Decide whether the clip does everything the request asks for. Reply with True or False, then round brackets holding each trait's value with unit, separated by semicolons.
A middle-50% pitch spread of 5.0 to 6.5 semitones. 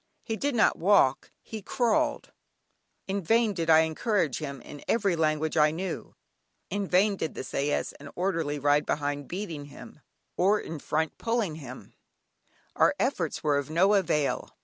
True (5.5 semitones)